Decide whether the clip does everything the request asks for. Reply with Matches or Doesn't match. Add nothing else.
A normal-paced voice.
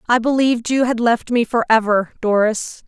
Matches